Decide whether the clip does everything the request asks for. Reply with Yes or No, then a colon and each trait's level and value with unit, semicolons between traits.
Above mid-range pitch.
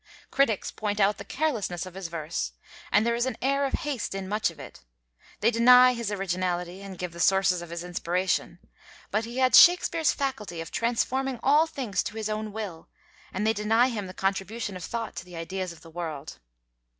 Yes: high, 210 Hz